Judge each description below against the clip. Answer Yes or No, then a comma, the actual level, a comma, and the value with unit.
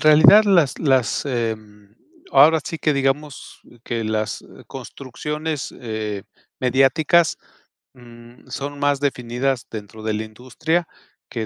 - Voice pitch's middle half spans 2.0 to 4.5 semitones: No, average, 5.0 semitones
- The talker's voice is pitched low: Yes, low, 130 Hz